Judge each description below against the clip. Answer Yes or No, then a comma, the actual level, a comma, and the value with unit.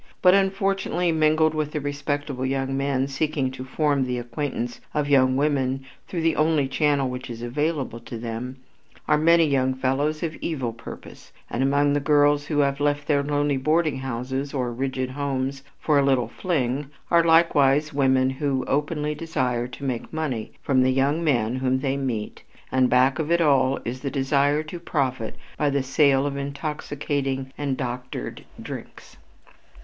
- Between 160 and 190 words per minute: Yes, average, 170 wpm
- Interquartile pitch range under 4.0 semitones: Yes, narrow, 2.4 semitones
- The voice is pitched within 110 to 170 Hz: Yes, medium, 140 Hz